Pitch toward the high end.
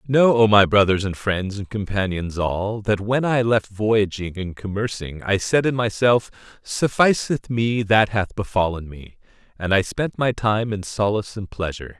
No: low, 105 Hz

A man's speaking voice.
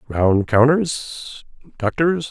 Yes: male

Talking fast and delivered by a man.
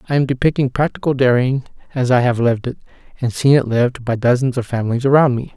Yes: fast, 215 wpm; male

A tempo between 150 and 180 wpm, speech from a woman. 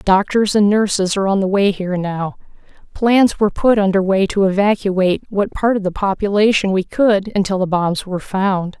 No: average, 190 wpm; female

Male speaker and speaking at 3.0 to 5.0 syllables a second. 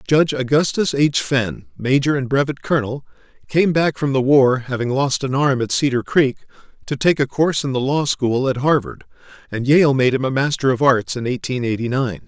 No: male; 5.3 syllables/s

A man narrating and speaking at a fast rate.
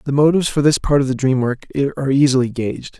Yes: male; fast, 240 wpm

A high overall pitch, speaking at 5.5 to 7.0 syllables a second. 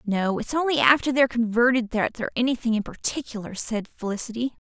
Yes: high, 235 Hz; 6.1 syllables/s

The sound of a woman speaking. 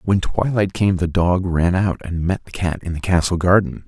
No: male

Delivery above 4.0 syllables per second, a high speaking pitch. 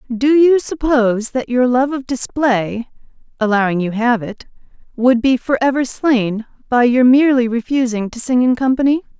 Yes: 4.8 syllables/s; very high, 250 Hz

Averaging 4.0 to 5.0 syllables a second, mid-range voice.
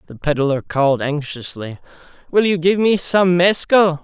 Yes: 4.5 syllables/s; medium, 165 Hz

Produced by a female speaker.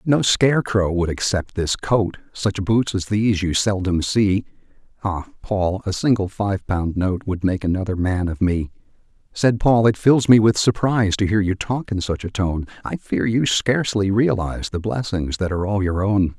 No: male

